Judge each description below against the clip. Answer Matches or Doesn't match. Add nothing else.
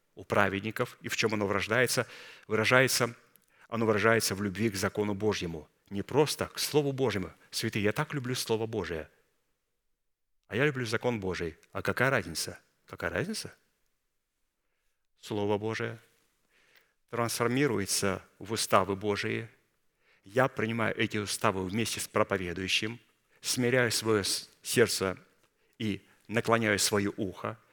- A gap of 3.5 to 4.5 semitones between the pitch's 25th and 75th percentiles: Doesn't match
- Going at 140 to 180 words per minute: Doesn't match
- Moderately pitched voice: Doesn't match